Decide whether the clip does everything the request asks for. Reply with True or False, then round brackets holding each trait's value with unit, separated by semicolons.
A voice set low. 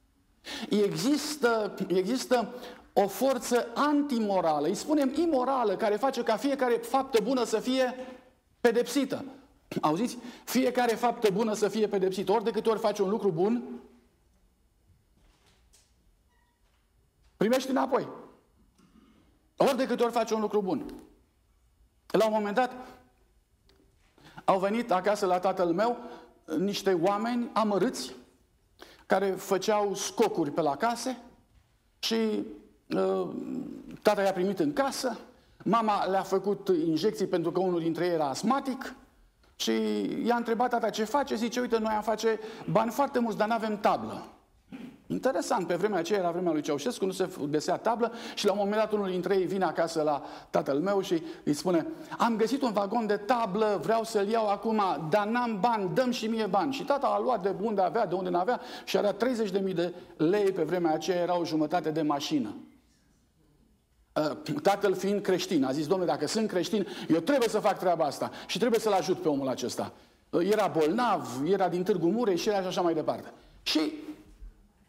False (215 Hz)